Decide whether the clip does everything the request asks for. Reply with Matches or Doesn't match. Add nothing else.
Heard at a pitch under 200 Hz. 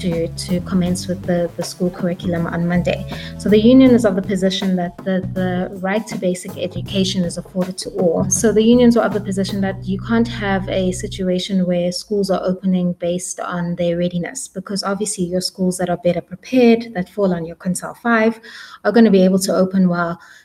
Matches